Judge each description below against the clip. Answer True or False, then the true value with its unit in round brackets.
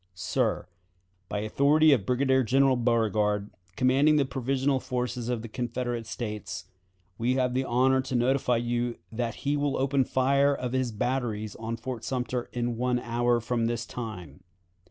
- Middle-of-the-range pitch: False (125 Hz)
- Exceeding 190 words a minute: False (160 wpm)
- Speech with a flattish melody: True (2.2 semitones)